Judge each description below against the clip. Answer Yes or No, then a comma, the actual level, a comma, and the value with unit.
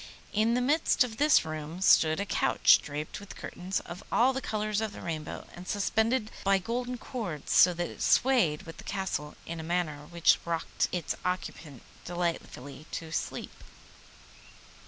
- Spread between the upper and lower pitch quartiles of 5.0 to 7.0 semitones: Yes, wide, 5.5 semitones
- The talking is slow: No, average, 165 wpm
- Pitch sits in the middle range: Yes, medium, 180 Hz